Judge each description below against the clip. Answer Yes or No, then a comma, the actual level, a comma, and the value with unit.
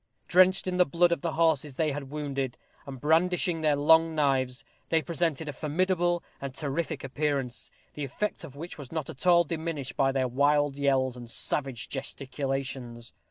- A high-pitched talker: No, medium, 145 Hz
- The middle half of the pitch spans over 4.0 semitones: No, average, 3.5 semitones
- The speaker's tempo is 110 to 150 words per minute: No, average, 170 wpm